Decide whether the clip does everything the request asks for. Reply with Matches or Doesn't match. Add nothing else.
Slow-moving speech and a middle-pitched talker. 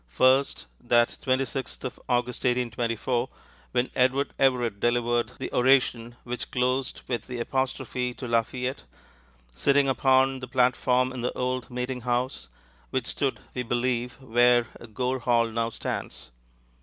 Doesn't match